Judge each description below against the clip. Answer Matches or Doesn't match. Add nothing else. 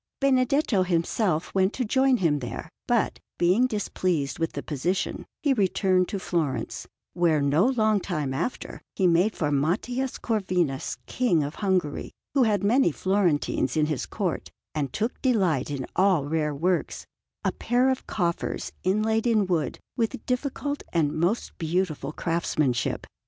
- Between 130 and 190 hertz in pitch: Matches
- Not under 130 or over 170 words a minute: Matches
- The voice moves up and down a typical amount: Doesn't match